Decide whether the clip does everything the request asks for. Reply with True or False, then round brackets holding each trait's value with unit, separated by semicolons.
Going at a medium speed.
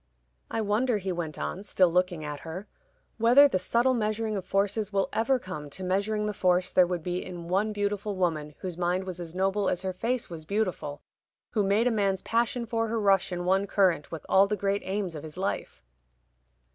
False (210 wpm)